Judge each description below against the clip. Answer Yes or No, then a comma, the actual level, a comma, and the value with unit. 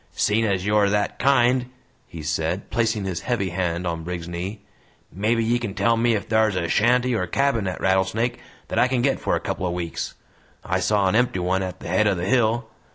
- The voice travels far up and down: No, average, 4.4 semitones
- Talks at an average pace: No, fast, 220 wpm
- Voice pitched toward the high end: No, low, 105 Hz